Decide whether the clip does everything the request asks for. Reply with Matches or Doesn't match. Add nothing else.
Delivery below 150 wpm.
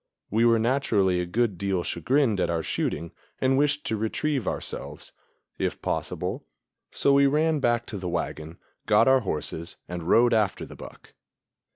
Doesn't match